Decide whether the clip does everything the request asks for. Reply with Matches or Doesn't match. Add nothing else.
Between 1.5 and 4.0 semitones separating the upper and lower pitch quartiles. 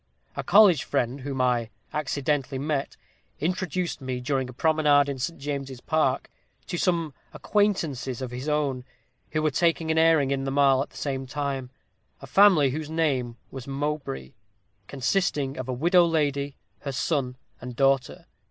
Matches